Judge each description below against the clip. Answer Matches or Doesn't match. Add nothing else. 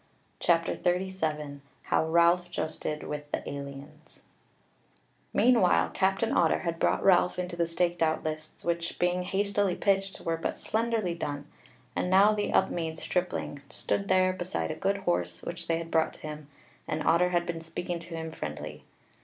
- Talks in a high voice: Doesn't match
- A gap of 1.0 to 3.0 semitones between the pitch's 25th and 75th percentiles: Matches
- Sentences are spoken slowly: Doesn't match